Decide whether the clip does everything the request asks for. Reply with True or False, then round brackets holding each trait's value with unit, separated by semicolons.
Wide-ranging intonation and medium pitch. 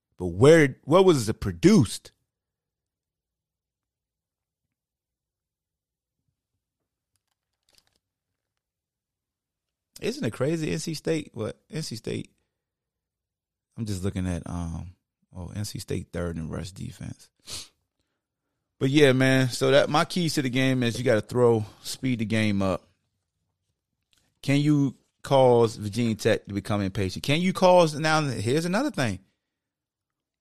False (6.9 semitones; 120 Hz)